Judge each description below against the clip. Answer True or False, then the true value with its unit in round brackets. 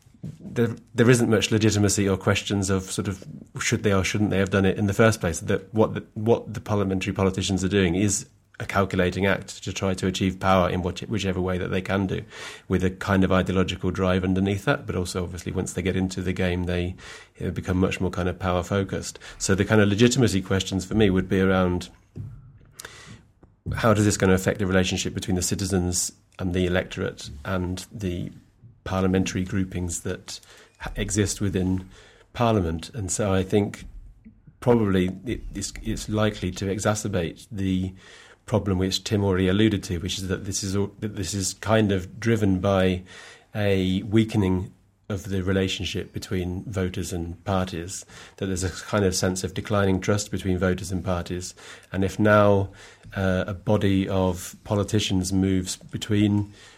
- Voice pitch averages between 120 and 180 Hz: False (95 Hz)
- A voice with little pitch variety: True (2.0 semitones)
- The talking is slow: False (185 wpm)